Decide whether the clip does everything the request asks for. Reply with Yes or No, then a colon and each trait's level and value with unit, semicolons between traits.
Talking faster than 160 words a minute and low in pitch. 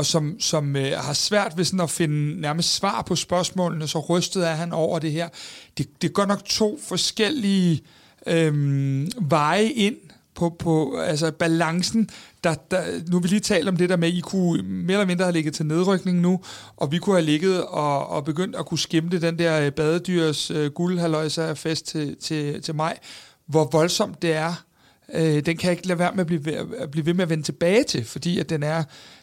No: average, 210 wpm; medium, 170 Hz